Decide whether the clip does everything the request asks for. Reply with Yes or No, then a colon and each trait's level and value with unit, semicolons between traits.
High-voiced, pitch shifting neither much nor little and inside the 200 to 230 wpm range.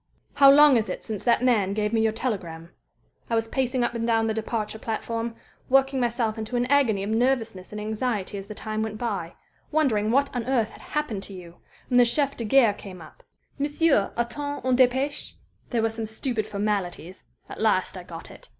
Yes: high, 225 Hz; average, 3.2 semitones; fast, 205 wpm